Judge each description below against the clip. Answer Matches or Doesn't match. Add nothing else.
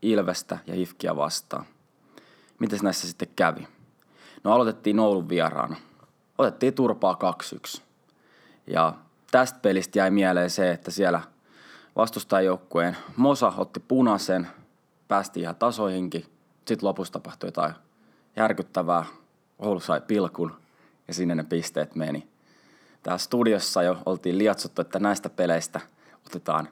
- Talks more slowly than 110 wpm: Doesn't match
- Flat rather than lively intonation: Doesn't match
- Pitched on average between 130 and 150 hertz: Doesn't match